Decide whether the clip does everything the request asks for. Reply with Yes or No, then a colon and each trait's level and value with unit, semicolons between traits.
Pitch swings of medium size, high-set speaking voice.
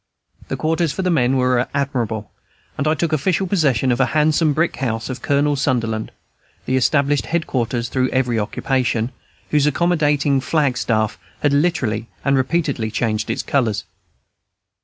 No: average, 4.0 semitones; low, 135 Hz